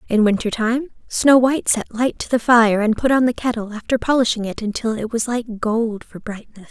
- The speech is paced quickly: Yes, fast, 225 wpm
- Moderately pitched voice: No, high, 230 Hz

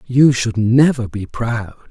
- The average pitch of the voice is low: Yes, low, 120 Hz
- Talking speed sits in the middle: Yes, average, 160 wpm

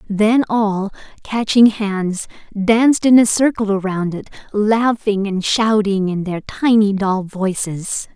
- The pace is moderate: No, slow, 130 wpm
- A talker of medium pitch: No, high, 205 Hz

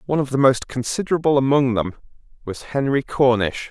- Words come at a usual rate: Yes, average, 160 wpm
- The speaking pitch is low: Yes, low, 130 Hz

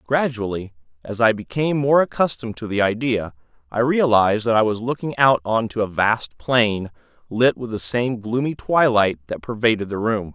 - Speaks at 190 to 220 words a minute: No, average, 180 wpm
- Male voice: Yes, male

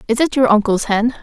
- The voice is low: No, high, 235 Hz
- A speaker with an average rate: No, fast, 245 wpm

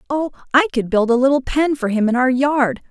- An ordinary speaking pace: No, fast, 250 wpm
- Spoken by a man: No, female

